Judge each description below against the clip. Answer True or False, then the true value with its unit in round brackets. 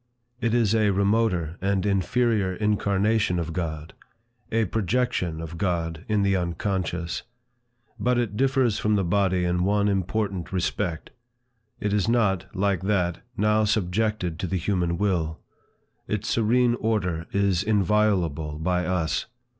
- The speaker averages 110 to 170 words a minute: True (135 wpm)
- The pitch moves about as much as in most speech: True (3.4 semitones)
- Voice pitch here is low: True (100 Hz)